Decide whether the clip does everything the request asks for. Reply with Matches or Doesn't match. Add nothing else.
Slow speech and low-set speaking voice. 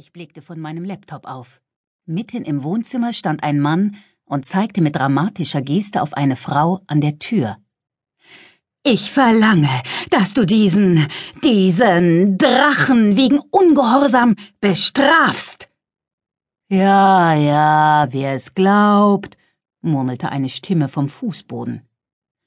Doesn't match